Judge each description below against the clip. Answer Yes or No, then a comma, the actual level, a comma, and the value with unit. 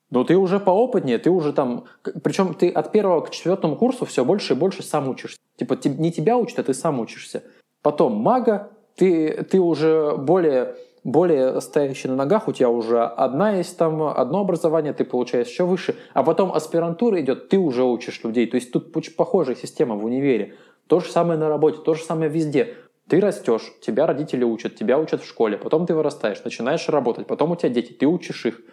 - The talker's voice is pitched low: No, medium, 160 Hz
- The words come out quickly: Yes, fast, 200 wpm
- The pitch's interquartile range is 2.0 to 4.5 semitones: No, average, 5.0 semitones